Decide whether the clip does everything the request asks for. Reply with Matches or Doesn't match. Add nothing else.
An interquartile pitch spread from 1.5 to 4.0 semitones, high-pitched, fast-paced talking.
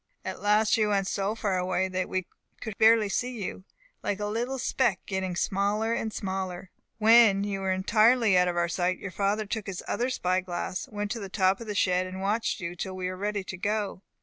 Matches